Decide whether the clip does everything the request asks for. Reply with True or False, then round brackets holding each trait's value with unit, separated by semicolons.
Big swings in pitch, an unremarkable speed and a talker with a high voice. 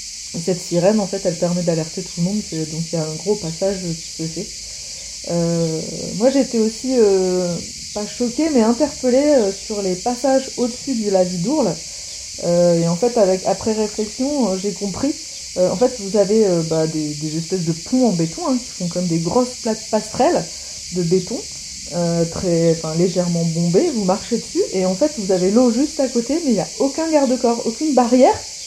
True (6.0 semitones; 200 wpm; 195 Hz)